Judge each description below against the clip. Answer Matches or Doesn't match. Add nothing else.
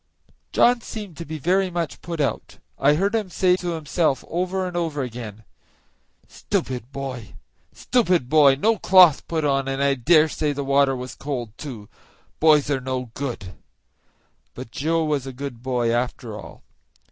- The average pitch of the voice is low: Doesn't match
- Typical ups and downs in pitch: Matches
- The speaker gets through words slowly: Doesn't match